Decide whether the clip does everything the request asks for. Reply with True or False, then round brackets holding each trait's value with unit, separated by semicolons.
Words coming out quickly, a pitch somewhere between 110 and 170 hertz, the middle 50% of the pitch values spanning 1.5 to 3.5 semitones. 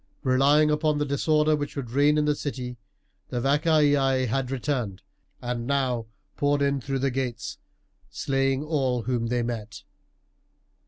False (145 wpm; 135 Hz; 2.9 semitones)